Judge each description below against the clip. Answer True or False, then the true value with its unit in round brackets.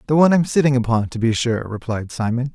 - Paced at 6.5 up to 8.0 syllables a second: False (6.3 syllables/s)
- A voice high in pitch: False (125 Hz)